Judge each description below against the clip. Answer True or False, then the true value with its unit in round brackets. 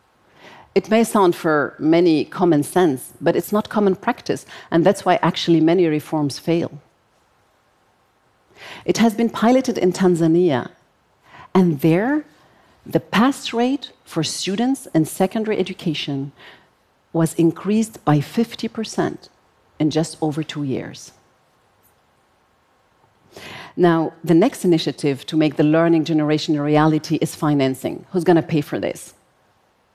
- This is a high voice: False (170 Hz)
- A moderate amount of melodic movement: True (4.8 semitones)